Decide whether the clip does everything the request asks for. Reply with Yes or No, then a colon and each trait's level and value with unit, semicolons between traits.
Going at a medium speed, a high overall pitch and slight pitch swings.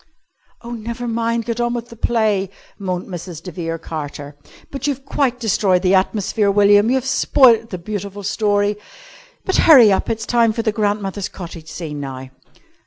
No: average, 170 wpm; high, 205 Hz; average, 4.2 semitones